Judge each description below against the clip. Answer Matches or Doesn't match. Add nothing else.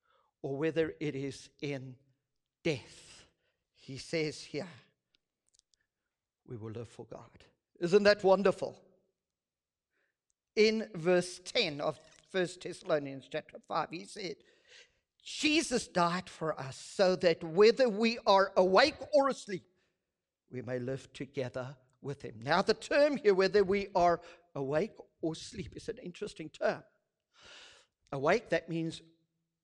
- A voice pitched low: Doesn't match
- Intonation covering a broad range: Matches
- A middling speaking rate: Doesn't match